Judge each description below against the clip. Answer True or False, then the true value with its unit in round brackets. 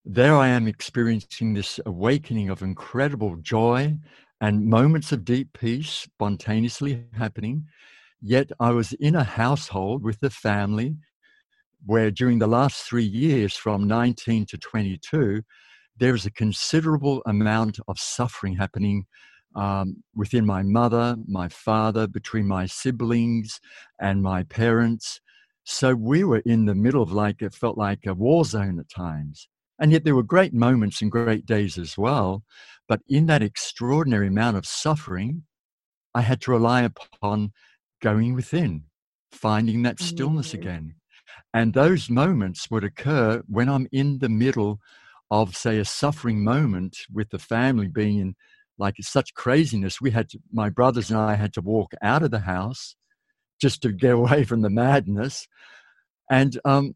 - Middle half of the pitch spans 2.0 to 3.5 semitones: False (4.3 semitones)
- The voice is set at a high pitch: False (115 Hz)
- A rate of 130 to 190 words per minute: True (155 wpm)